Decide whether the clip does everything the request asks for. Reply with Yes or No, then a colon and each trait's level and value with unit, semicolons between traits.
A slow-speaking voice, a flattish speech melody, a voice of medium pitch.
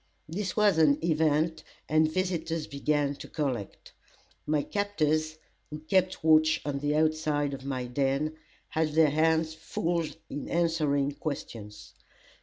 Yes: slow, 130 wpm; narrow, 2.0 semitones; medium, 155 Hz